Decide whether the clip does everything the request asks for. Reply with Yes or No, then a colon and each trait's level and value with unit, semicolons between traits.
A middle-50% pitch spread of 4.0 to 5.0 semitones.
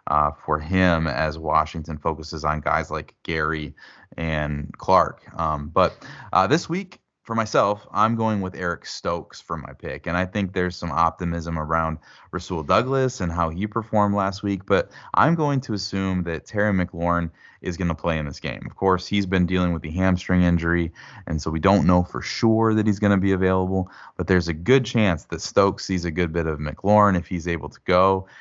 No: average, 3.4 semitones